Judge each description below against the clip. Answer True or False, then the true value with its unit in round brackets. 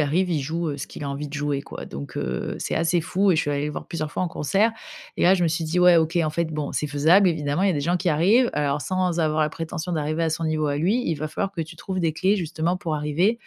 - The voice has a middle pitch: True (160 Hz)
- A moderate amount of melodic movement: True (3.0 semitones)